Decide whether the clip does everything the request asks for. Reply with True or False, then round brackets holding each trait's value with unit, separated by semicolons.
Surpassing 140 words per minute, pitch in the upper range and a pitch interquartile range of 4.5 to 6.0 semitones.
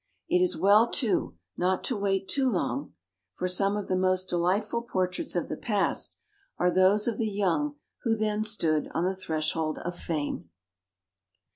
False (165 wpm; 195 Hz; 3.3 semitones)